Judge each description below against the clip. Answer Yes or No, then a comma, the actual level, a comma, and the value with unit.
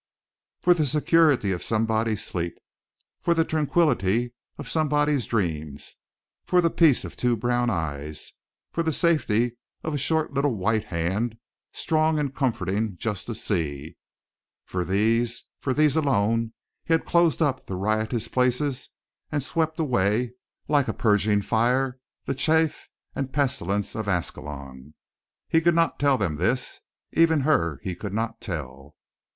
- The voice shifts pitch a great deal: Yes, wide, 7.0 semitones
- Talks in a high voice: No, low, 120 Hz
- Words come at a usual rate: Yes, average, 145 wpm